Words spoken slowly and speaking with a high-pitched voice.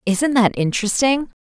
Yes: slow, 125 wpm; high, 235 Hz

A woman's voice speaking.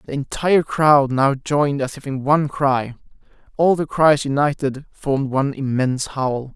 No: male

